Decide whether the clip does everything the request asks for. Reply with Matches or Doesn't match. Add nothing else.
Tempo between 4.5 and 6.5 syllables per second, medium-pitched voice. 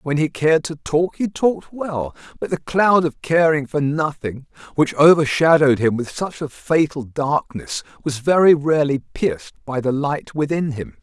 Matches